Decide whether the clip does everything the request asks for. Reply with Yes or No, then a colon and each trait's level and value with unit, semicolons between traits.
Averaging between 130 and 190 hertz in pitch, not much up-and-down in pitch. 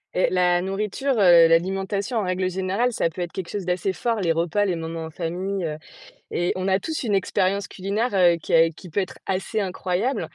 Yes: medium, 185 Hz; narrow, 2.3 semitones